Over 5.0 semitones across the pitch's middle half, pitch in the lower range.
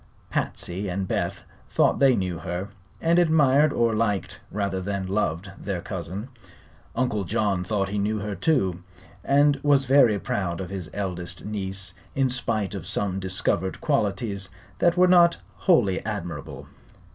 Yes: wide, 5.4 semitones; low, 100 Hz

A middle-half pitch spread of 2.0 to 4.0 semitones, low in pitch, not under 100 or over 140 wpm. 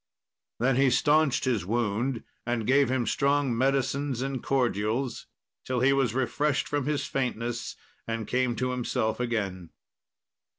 Yes: average, 2.7 semitones; low, 125 Hz; slow, 135 wpm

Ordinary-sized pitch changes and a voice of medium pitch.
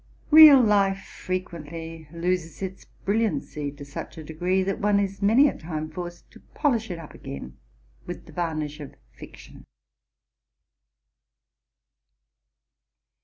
Yes: average, 4.1 semitones; medium, 175 Hz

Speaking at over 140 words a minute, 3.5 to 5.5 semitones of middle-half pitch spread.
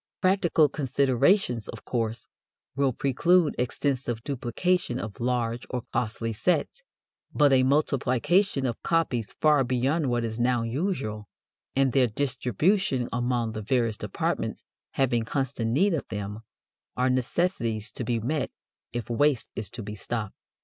No: slow, 135 wpm; average, 3.9 semitones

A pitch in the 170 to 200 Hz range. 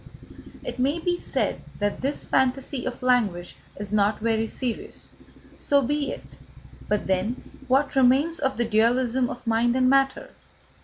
No: very high, 250 Hz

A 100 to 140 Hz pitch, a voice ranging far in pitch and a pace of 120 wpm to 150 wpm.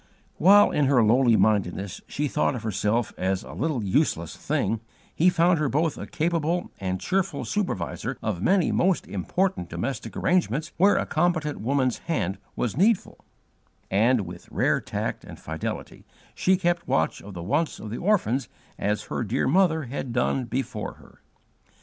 No: low, 135 Hz; wide, 8.3 semitones; average, 160 wpm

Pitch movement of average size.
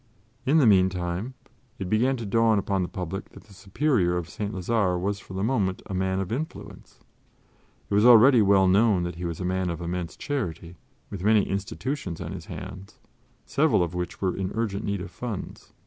Yes: average, 3.6 semitones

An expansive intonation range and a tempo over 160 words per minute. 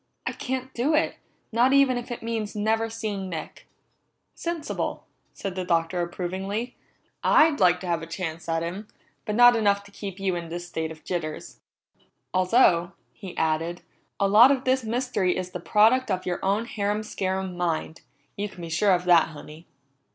No: average, 4.6 semitones; average, 180 wpm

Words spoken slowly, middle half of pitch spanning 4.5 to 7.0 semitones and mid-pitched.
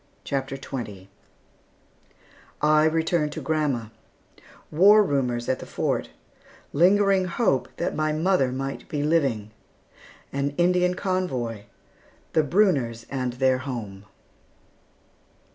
Yes: slow, 105 wpm; average, 5.3 semitones; medium, 145 Hz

